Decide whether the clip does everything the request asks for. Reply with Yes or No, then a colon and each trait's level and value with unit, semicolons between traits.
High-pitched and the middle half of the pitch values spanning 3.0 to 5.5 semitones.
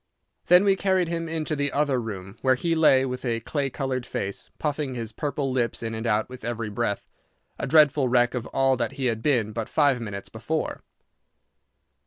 No: low, 130 Hz; average, 4.3 semitones